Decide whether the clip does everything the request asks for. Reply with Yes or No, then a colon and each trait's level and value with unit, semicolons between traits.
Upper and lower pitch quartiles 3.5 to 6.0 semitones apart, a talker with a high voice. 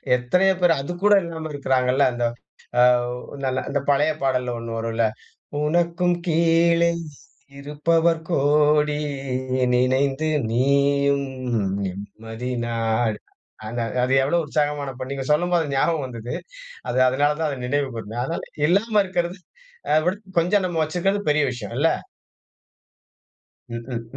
No: average, 4.9 semitones; medium, 140 Hz